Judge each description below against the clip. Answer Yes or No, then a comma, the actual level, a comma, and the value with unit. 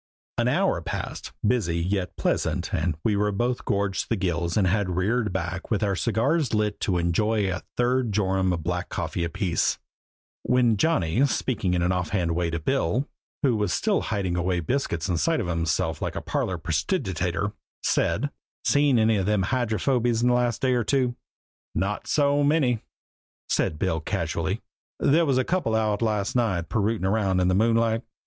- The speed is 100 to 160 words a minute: No, average, 175 wpm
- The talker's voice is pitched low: Yes, low, 105 Hz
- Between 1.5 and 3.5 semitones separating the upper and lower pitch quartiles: No, average, 5.0 semitones